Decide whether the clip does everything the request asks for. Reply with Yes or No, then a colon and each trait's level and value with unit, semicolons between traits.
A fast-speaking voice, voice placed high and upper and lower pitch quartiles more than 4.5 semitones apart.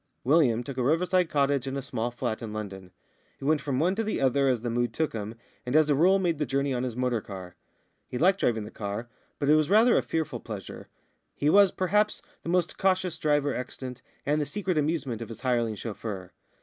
No: fast, 225 wpm; low, 135 Hz; wide, 5.6 semitones